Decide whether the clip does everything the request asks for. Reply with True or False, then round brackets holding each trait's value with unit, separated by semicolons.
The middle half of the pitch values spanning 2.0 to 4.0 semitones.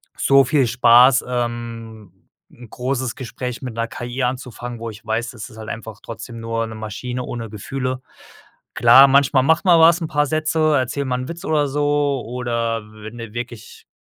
True (2.9 semitones)